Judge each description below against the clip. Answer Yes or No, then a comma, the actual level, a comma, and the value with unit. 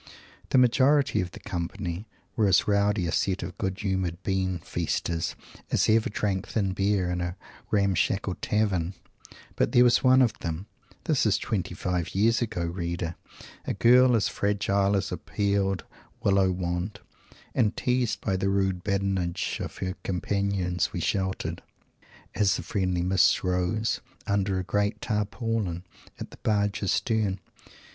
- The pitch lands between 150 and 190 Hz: No, very low, 95 Hz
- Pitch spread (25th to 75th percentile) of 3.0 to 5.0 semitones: No, narrow, 2.5 semitones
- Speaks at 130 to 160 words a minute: Yes, average, 150 wpm